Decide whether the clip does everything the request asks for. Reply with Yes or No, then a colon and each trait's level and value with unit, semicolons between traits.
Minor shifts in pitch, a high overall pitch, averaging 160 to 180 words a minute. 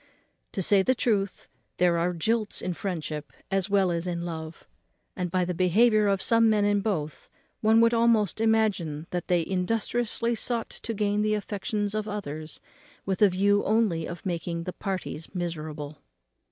No: average, 3.8 semitones; high, 195 Hz; average, 165 wpm